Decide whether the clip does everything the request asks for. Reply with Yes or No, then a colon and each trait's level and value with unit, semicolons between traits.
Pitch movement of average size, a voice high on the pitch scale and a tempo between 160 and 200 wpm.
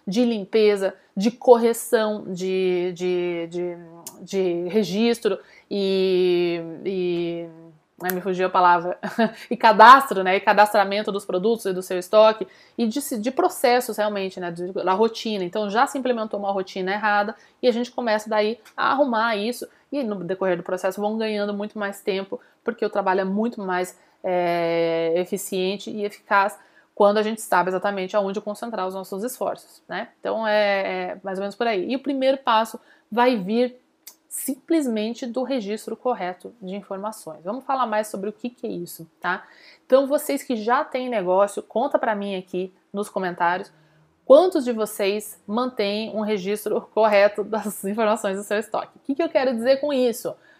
Yes: average, 3.7 semitones; high, 210 Hz; average, 165 wpm